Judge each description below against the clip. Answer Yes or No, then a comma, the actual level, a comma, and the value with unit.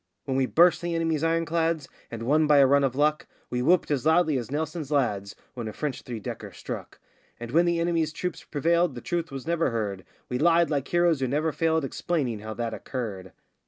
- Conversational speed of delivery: No, fast, 210 wpm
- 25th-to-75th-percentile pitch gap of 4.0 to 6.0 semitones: Yes, average, 4.9 semitones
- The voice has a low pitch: No, medium, 150 Hz